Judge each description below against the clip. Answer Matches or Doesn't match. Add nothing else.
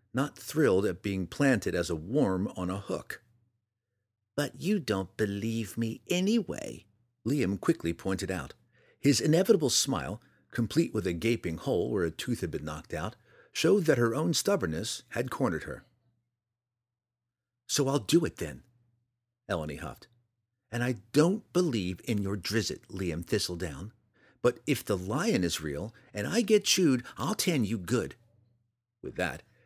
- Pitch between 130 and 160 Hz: Doesn't match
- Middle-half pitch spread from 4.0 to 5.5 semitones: Matches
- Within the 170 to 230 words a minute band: Doesn't match